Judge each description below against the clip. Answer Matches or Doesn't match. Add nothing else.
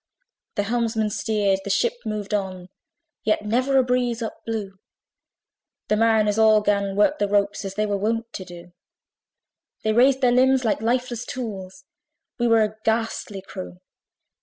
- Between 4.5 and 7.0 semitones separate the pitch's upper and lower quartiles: Doesn't match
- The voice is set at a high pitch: Matches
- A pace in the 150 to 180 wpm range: Matches